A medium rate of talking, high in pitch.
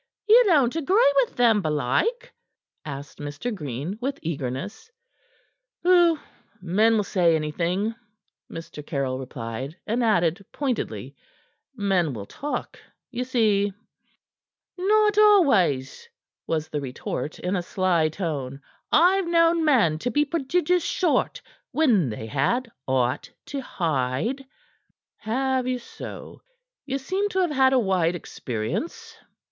No: slow, 120 wpm; high, 210 Hz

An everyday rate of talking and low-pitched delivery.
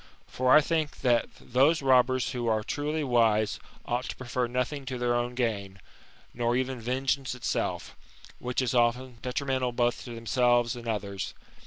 Yes: average, 160 wpm; low, 125 Hz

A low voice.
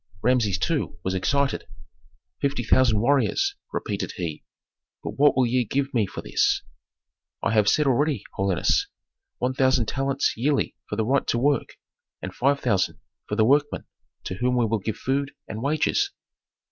Yes: low, 125 Hz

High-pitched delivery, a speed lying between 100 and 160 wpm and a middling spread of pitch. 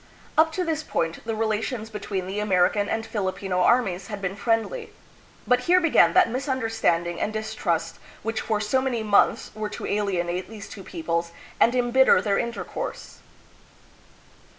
Yes: high, 215 Hz; average, 150 wpm; average, 4.2 semitones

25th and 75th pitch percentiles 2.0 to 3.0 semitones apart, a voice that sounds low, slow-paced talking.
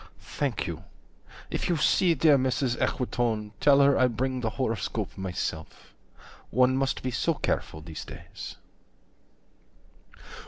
No: average, 3.8 semitones; low, 130 Hz; slow, 125 wpm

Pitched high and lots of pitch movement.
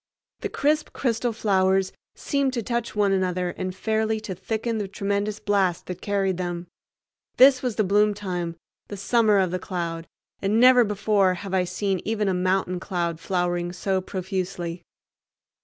No: high, 195 Hz; average, 2.9 semitones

